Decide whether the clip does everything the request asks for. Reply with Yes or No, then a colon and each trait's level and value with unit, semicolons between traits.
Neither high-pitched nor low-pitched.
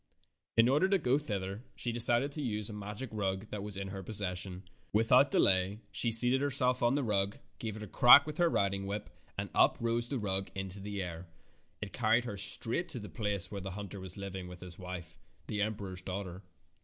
No: low, 105 Hz